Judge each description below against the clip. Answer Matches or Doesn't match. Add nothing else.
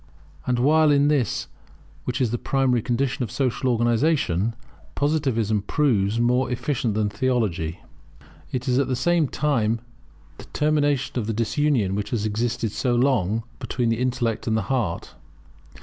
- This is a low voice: Matches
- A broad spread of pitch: Doesn't match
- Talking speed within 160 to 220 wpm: Doesn't match